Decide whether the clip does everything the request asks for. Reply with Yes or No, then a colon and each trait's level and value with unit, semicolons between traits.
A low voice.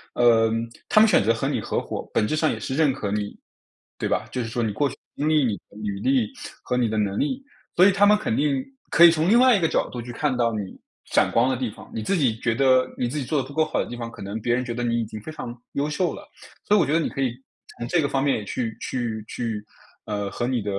Yes: low, 125 Hz